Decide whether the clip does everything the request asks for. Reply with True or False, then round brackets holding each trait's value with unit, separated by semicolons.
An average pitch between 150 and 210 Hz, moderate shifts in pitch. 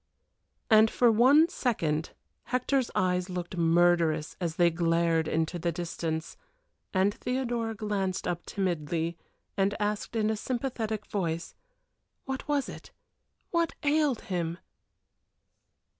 False (190 Hz; 5.7 semitones)